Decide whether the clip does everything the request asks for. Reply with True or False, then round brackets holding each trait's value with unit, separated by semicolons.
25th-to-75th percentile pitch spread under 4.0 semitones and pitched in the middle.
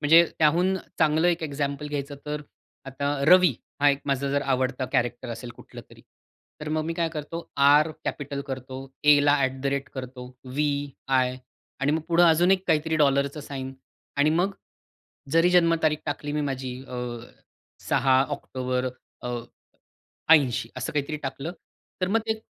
True (2.9 semitones; 145 Hz)